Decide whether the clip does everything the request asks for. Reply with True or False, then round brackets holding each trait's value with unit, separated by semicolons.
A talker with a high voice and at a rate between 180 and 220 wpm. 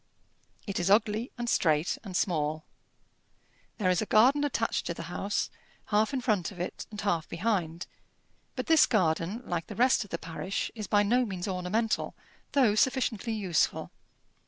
False (205 Hz; 165 wpm)